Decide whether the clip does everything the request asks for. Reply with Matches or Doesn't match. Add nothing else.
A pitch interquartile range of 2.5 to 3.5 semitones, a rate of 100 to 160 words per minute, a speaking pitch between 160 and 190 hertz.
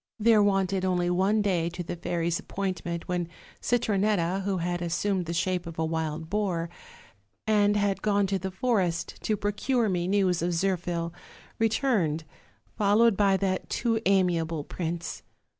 Matches